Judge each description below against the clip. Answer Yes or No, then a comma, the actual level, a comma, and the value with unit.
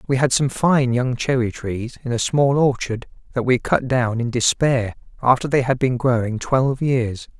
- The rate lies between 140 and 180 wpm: No, average, 195 wpm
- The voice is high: No, low, 125 Hz